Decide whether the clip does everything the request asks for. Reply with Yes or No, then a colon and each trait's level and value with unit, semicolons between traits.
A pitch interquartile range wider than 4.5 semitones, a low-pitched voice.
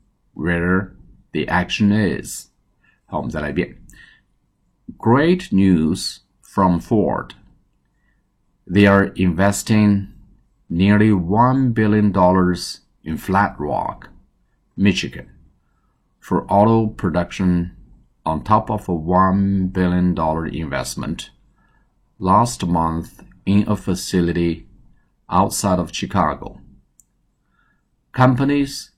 No: average, 3.2 semitones; very low, 95 Hz